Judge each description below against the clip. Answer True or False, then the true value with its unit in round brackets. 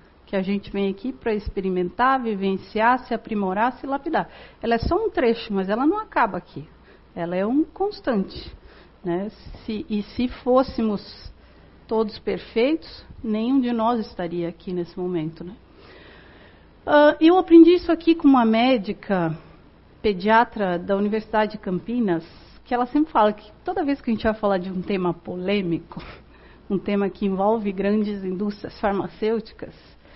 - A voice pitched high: True (215 Hz)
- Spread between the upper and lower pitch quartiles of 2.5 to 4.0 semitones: False (4.4 semitones)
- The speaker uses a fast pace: False (150 wpm)